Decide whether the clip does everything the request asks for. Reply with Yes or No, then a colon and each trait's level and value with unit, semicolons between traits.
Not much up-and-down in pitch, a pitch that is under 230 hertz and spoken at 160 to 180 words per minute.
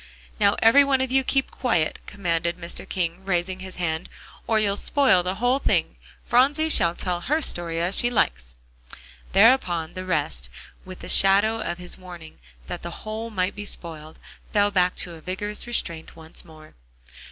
No: average, 4.5 semitones; medium, 185 Hz; average, 175 wpm